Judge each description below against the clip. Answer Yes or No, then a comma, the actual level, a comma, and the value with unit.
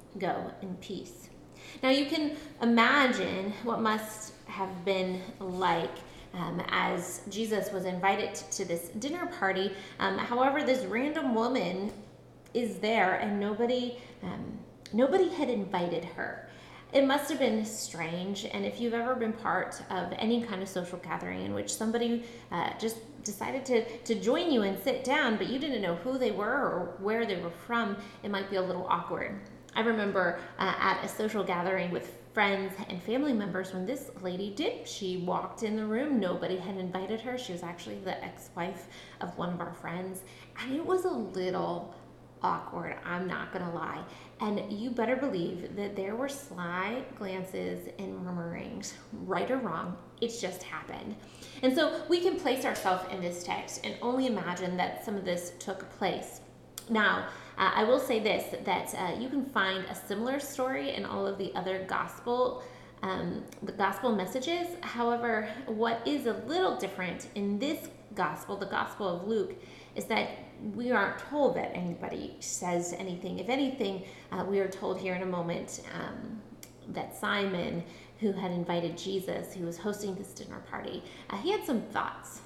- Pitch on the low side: No, high, 205 Hz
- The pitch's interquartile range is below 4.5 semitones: No, average, 4.9 semitones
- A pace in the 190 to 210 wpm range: No, average, 170 wpm